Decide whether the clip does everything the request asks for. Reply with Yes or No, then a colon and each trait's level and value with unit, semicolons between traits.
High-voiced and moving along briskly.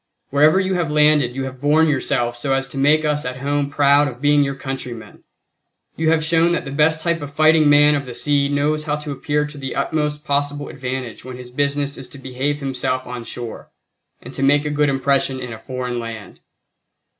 No: medium, 145 Hz; fast, 215 wpm